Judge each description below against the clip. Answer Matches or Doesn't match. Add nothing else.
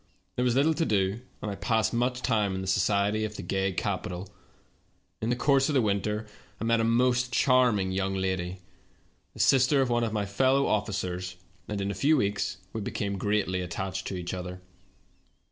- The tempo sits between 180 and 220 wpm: Matches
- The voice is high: Doesn't match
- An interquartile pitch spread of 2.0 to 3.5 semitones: Doesn't match